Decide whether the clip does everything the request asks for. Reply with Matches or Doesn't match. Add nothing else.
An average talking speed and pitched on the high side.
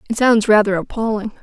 Matches